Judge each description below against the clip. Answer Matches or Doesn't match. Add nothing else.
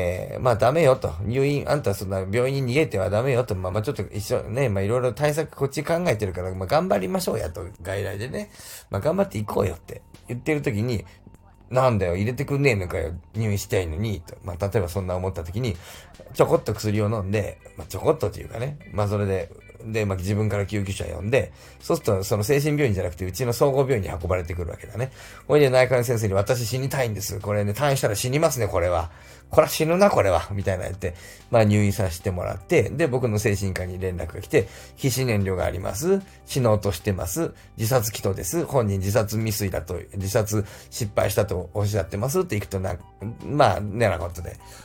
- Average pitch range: Matches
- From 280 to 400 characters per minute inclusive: Doesn't match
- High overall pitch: Doesn't match